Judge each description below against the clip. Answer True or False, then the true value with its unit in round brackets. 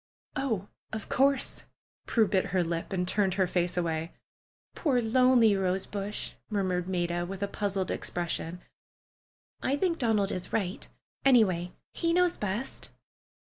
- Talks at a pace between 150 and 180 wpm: False (140 wpm)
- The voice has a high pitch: True (195 Hz)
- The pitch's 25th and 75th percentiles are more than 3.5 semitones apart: True (4.7 semitones)